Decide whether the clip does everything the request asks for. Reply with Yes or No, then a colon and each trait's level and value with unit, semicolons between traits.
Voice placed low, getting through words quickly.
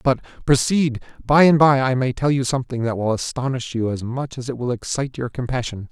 Yes: low, 130 Hz; fast, 225 wpm